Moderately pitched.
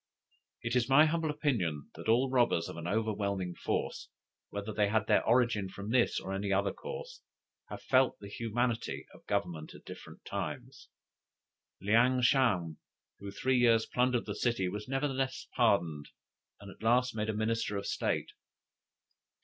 No: low, 115 Hz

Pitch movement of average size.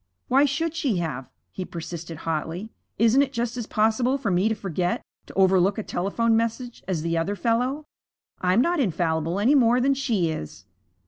No: wide, 6.2 semitones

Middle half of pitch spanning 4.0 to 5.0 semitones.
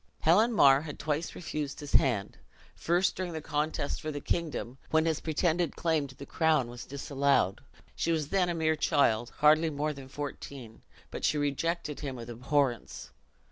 No: average, 2.8 semitones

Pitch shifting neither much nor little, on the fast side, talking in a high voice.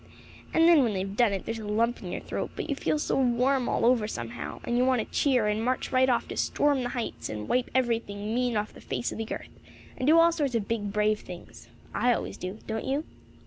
Yes: average, 3.6 semitones; fast, 255 wpm; high, 235 Hz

